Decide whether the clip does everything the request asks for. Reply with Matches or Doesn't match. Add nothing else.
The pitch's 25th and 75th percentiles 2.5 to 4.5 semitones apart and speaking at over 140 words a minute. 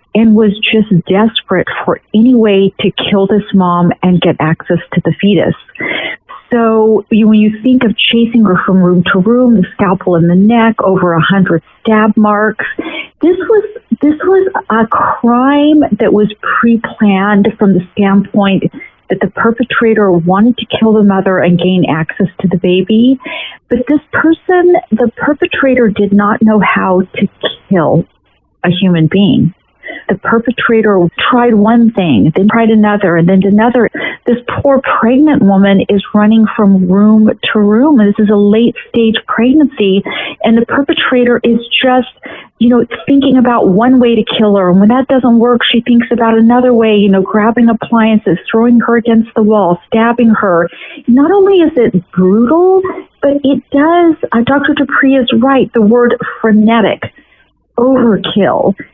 Matches